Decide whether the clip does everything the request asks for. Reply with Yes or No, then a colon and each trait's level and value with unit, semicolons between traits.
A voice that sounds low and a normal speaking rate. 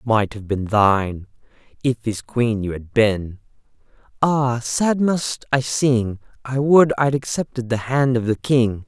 Yes: low, 120 Hz; average, 170 wpm